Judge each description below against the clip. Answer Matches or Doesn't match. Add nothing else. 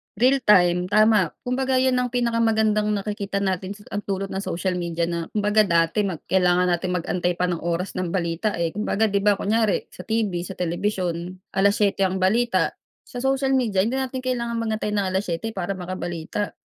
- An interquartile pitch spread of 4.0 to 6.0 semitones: Doesn't match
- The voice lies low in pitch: Doesn't match